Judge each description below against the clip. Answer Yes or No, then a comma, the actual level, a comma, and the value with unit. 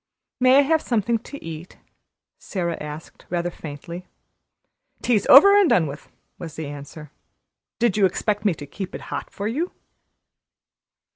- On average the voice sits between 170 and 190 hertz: Yes, medium, 185 Hz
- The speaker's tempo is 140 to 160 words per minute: Yes, average, 150 wpm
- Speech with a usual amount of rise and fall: No, wide, 7.0 semitones